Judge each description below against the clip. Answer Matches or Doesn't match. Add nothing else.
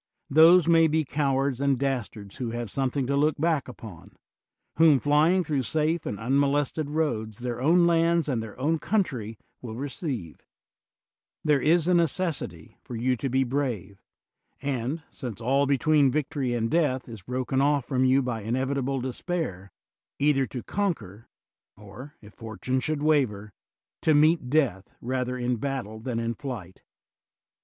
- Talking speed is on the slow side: Doesn't match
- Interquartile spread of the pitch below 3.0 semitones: Doesn't match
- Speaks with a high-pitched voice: Doesn't match